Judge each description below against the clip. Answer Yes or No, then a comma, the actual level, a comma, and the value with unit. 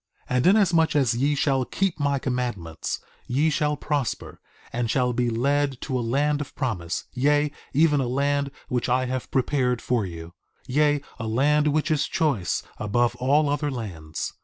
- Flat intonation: No, average, 3.4 semitones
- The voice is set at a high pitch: No, low, 135 Hz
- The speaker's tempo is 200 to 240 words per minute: No, average, 170 wpm